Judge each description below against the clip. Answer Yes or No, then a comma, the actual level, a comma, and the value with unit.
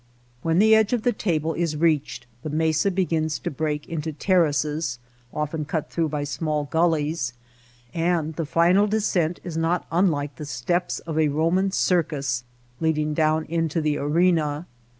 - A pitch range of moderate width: No, narrow, 2.3 semitones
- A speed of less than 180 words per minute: Yes, average, 155 wpm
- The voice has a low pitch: No, medium, 160 Hz